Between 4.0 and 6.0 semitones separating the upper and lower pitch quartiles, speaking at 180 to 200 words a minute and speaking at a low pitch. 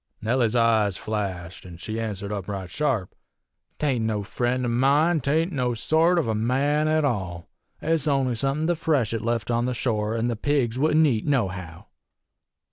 Yes: average, 5.1 semitones; average, 185 wpm; low, 120 Hz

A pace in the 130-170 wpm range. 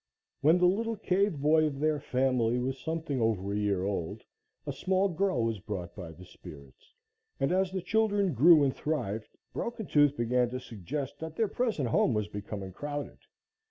No: average, 180 wpm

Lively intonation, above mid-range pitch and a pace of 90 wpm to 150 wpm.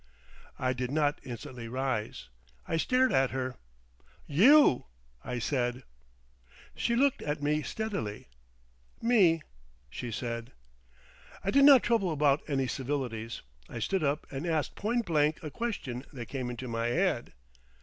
No: wide, 6.7 semitones; medium, 140 Hz; average, 140 wpm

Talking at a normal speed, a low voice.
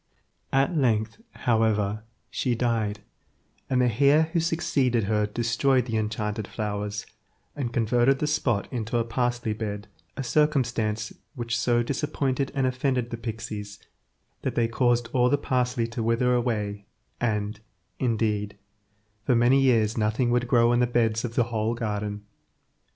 Yes: average, 145 wpm; low, 120 Hz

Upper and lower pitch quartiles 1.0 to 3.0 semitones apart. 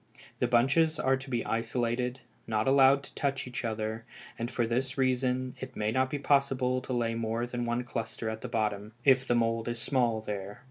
Yes: narrow, 2.5 semitones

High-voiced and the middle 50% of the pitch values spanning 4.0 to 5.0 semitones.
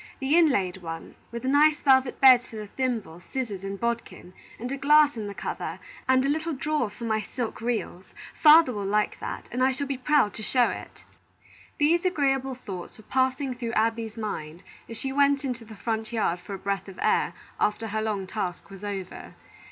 Yes: high, 235 Hz; average, 4.6 semitones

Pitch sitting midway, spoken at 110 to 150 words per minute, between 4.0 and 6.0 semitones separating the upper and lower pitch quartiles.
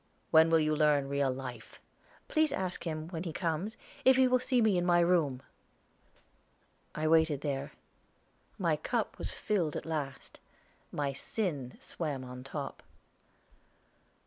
Yes: medium, 160 Hz; average, 145 wpm; average, 4.3 semitones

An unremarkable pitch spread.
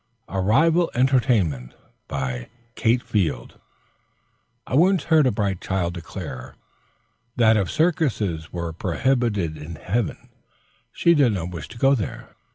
No: wide, 7.6 semitones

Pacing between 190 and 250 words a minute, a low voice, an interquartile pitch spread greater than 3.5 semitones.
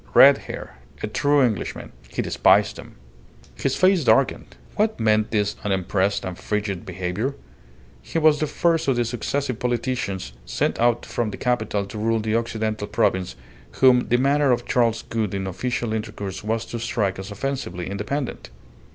No: average, 160 wpm; low, 110 Hz; average, 3.9 semitones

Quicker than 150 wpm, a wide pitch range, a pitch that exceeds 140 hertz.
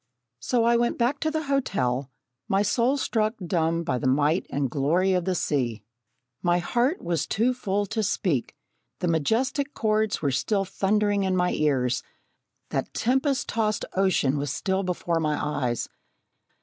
Yes: average, 160 wpm; wide, 7.1 semitones; high, 190 Hz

